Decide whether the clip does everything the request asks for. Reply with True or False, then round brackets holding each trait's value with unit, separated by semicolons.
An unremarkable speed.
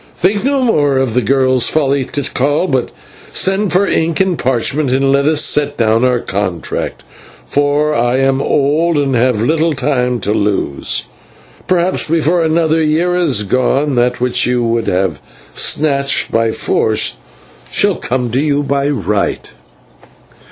True (150 wpm)